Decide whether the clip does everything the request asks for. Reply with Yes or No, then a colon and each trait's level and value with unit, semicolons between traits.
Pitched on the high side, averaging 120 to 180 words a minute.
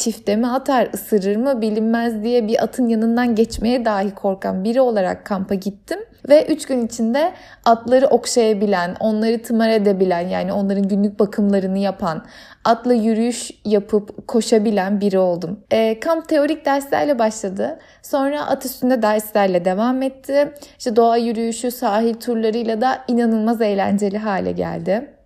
Yes: high, 225 Hz; fast, 140 wpm